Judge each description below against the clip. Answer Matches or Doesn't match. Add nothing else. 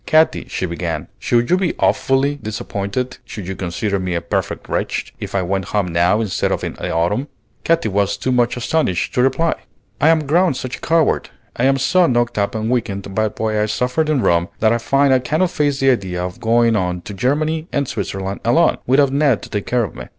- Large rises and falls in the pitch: Matches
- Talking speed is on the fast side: Matches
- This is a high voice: Doesn't match